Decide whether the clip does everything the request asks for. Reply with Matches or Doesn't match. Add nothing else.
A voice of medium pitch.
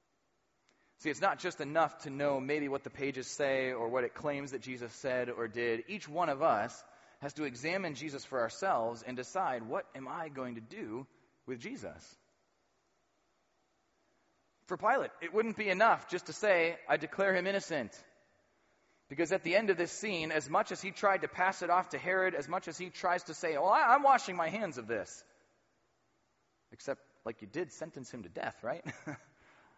Matches